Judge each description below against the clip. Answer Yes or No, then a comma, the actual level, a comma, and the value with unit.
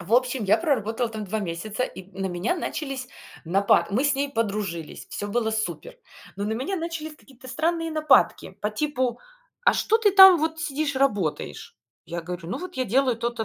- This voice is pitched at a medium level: No, very high, 250 Hz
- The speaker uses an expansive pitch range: Yes, wide, 7.0 semitones